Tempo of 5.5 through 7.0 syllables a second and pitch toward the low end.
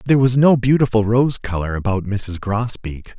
No: 5.0 syllables/s; low, 110 Hz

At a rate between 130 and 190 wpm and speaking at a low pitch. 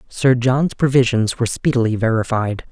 Yes: slow, 135 wpm; low, 120 Hz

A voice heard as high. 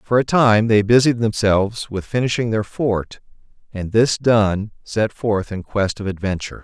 No: low, 110 Hz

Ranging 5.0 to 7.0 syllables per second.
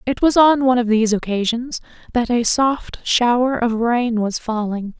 No: 4.7 syllables/s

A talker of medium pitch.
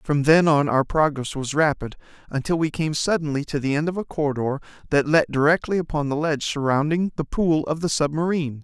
Yes: medium, 150 Hz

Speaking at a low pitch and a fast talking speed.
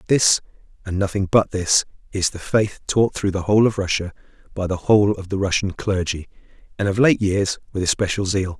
No: low, 100 Hz; average, 195 wpm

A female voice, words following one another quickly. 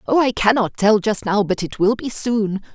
Yes: female; fast, 240 wpm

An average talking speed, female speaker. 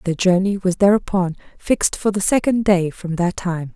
Yes: average, 190 wpm; female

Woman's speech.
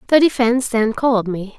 Yes: female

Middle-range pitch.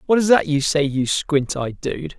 Yes: medium, 155 Hz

